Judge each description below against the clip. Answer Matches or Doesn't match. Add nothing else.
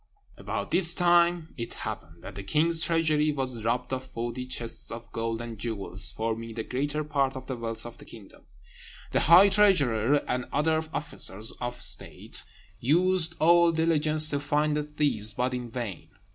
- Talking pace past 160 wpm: Matches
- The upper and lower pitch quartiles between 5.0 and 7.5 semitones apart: Matches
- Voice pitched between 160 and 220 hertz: Doesn't match